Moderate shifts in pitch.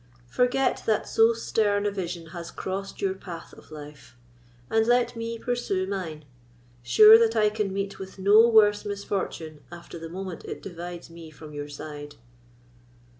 Yes: average, 4.7 semitones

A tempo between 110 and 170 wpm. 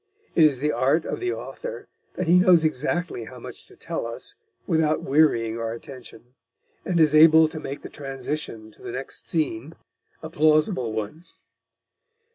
Yes: average, 165 wpm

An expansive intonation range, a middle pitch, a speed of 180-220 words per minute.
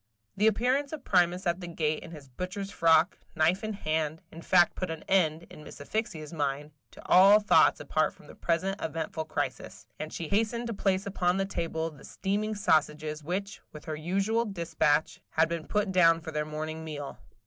No: average, 3.9 semitones; medium, 170 Hz; average, 190 wpm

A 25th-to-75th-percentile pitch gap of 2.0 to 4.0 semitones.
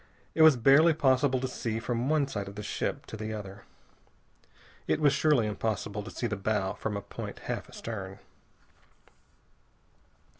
No: average, 4.6 semitones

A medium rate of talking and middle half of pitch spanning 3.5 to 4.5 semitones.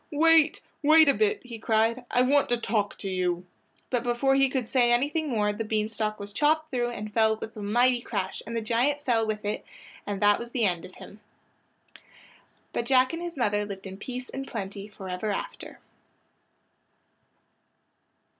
Yes: average, 185 wpm; average, 3.9 semitones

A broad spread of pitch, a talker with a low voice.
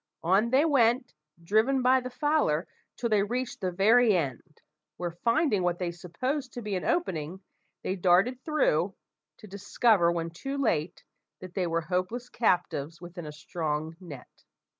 No: wide, 6.3 semitones; high, 190 Hz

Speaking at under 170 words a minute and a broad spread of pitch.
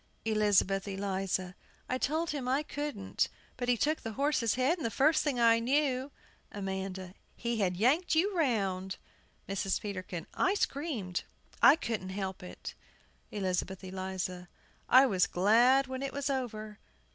Yes: average, 145 wpm; wide, 6.1 semitones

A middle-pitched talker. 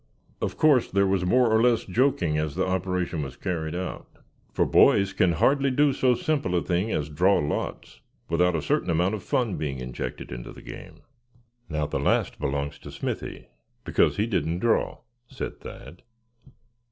No: very low, 90 Hz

